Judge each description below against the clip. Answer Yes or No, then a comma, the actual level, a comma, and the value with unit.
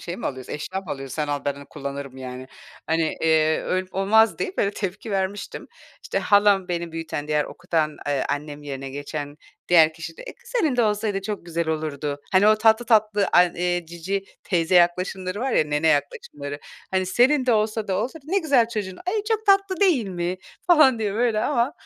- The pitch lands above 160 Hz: Yes, medium, 185 Hz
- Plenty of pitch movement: Yes, wide, 6.2 semitones